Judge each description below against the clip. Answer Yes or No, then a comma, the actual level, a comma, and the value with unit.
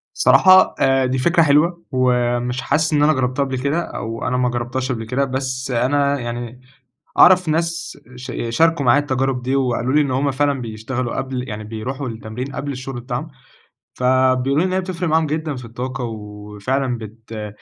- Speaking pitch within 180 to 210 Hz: No, low, 130 Hz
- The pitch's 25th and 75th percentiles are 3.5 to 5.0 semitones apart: No, average, 2.9 semitones